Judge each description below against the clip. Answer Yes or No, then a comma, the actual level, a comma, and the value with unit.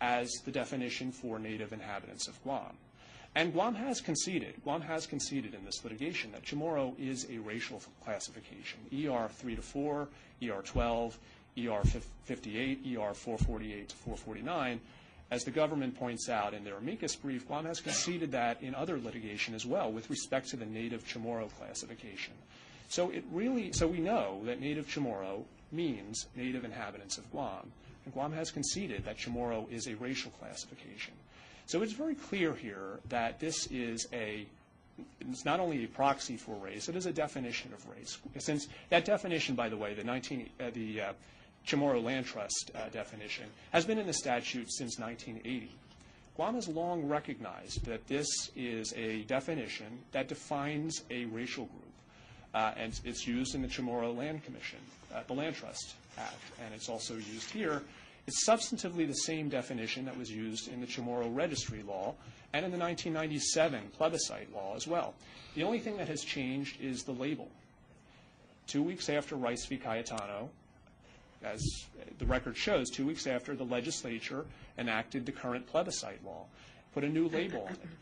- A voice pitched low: Yes, low, 130 Hz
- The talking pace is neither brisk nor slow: Yes, average, 170 wpm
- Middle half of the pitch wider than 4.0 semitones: Yes, average, 4.9 semitones